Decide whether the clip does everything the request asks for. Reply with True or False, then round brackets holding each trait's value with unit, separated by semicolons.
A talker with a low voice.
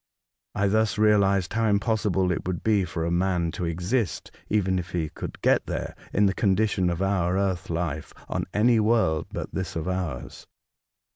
True (95 Hz)